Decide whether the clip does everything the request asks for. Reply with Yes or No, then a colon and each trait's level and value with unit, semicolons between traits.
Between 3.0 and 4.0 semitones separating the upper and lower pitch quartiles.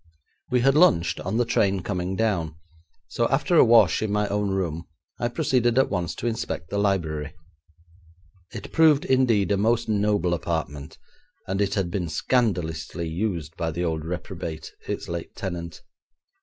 No: average, 5.2 semitones